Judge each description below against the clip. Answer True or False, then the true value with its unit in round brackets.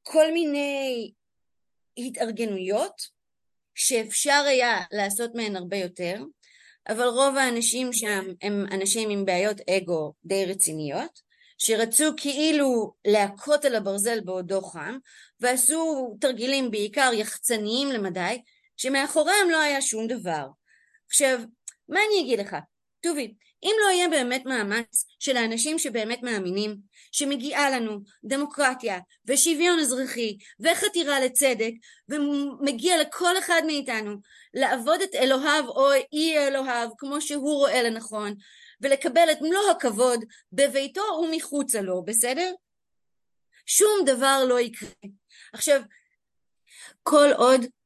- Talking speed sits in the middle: True (110 wpm)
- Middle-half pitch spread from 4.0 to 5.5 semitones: True (5.1 semitones)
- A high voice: True (255 Hz)